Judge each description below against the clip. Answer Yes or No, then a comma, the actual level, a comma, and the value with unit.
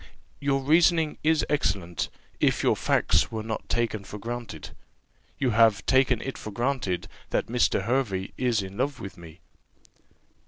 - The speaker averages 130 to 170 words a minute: Yes, average, 150 wpm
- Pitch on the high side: No, low, 115 Hz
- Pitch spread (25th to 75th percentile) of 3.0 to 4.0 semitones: No, average, 5.2 semitones